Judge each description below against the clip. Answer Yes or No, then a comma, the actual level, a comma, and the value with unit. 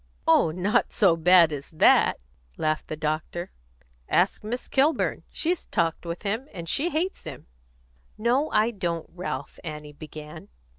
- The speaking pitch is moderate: Yes, medium, 175 Hz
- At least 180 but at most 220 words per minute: No, average, 145 wpm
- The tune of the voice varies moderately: No, wide, 6.7 semitones